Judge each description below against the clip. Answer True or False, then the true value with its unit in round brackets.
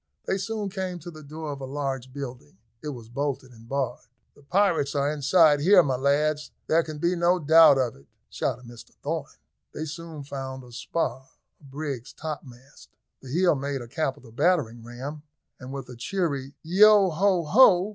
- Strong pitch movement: False (4.2 semitones)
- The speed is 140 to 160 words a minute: False (180 wpm)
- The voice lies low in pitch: False (145 Hz)